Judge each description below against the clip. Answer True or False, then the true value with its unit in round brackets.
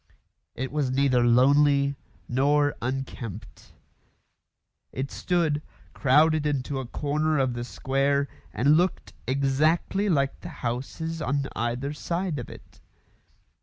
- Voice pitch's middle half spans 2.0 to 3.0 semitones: True (2.6 semitones)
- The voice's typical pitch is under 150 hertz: True (140 Hz)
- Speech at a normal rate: False (115 wpm)